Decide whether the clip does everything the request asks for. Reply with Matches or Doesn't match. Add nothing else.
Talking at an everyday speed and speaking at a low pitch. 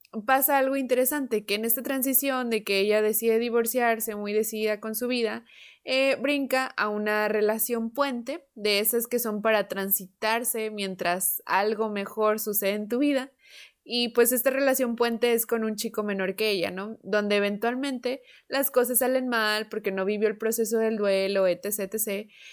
Doesn't match